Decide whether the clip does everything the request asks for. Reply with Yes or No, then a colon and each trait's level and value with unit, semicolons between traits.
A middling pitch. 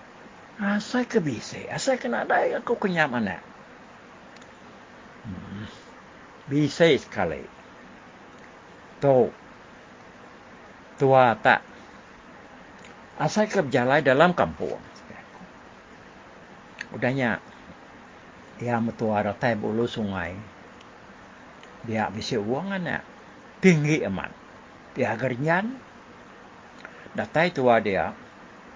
Yes: medium, 150 Hz